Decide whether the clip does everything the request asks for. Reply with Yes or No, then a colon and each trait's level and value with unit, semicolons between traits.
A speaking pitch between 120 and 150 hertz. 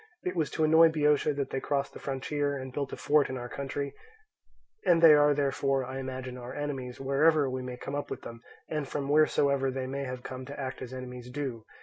Yes: medium, 140 Hz